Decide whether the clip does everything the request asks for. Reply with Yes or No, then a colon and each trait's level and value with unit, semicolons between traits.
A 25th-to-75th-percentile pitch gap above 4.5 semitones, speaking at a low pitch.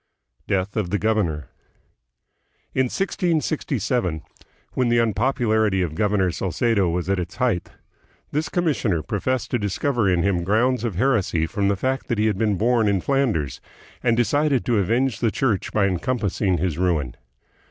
Yes: average, 5.2 semitones; low, 105 Hz